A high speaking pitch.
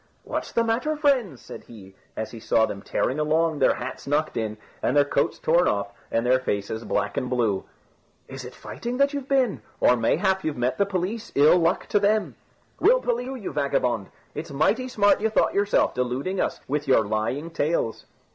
No: medium, 150 Hz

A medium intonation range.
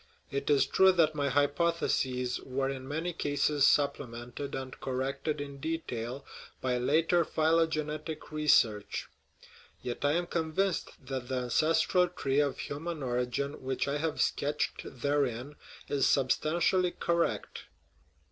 Yes: average, 3.4 semitones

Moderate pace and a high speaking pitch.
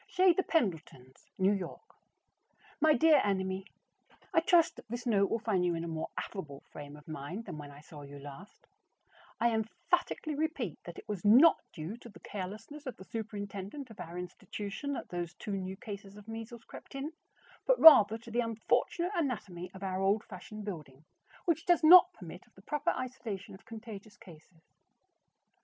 Yes: average, 180 wpm; high, 205 Hz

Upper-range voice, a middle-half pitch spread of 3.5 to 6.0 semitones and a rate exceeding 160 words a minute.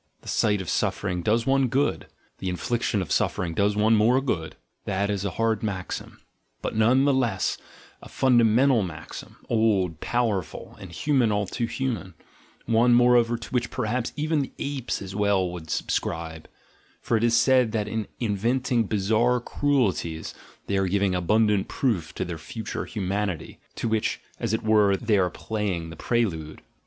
No: low, 110 Hz; average, 4.0 semitones; average, 170 wpm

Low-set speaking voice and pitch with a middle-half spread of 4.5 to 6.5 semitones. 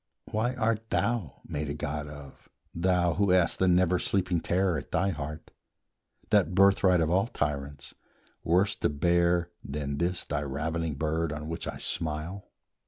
No: very low, 85 Hz; average, 3.6 semitones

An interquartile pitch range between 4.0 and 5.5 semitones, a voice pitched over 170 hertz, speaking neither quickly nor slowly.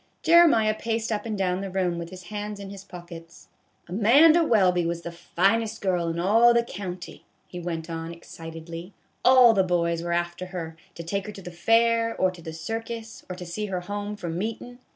No: average, 4.4 semitones; medium, 185 Hz; fast, 210 wpm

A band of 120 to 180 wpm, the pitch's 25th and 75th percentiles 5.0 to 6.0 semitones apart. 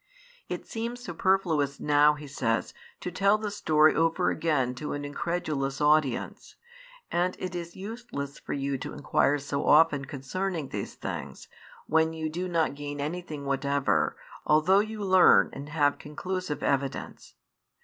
No: average, 145 wpm; average, 4.1 semitones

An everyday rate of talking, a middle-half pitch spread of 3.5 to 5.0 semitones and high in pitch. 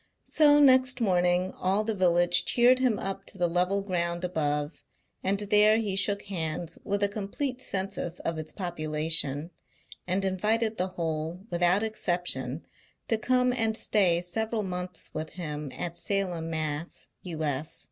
No: average, 145 wpm; average, 3.9 semitones; medium, 180 Hz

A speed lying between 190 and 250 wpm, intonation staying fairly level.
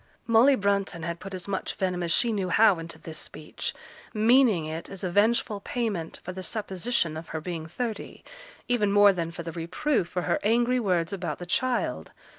No: average, 195 wpm; average, 4.7 semitones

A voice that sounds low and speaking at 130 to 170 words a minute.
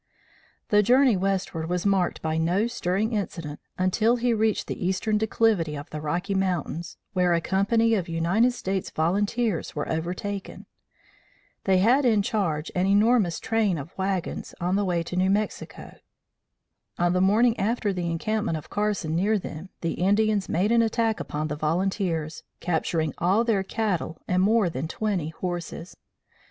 No: high, 190 Hz; average, 160 wpm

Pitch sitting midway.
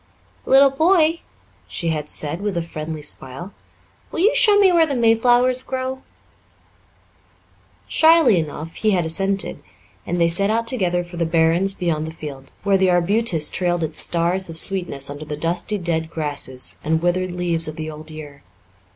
Yes: medium, 175 Hz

